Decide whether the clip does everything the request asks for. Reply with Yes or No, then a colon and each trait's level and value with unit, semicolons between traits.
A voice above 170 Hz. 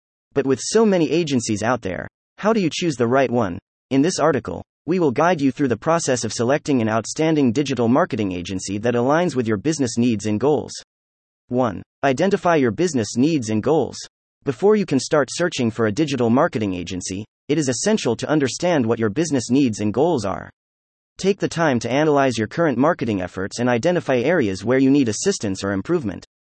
No: low, 125 Hz